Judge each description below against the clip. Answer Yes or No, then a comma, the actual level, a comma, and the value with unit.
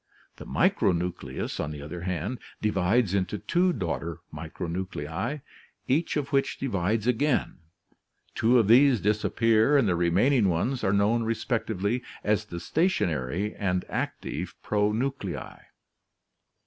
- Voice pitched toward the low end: Yes, low, 105 Hz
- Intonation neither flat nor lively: No, wide, 5.8 semitones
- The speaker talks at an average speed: No, slow, 120 wpm